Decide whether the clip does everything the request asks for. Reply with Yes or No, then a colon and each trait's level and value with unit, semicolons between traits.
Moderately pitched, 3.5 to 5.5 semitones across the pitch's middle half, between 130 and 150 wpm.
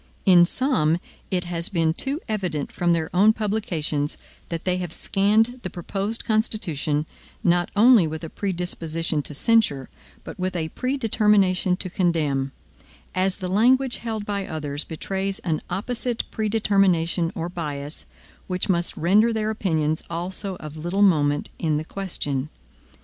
Yes: medium, 180 Hz; average, 4.6 semitones; average, 145 wpm